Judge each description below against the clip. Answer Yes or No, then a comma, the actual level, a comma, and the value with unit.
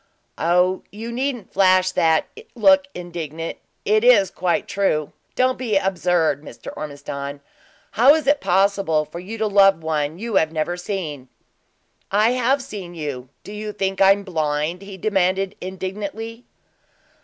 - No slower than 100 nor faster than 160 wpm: Yes, average, 145 wpm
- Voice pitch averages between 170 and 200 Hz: Yes, high, 190 Hz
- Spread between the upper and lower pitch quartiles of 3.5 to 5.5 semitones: Yes, average, 4.5 semitones